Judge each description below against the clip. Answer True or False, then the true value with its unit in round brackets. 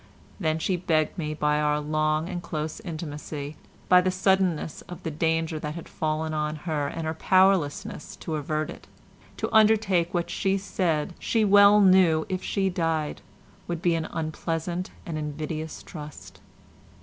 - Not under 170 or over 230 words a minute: False (160 wpm)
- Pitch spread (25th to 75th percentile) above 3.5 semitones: False (3.0 semitones)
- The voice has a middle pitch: True (160 Hz)